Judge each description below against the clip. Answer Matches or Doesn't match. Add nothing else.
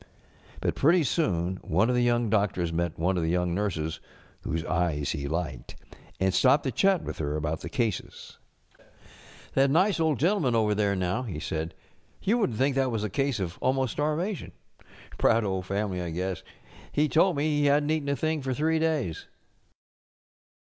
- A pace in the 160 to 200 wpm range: Matches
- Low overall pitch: Matches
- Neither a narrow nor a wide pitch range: Doesn't match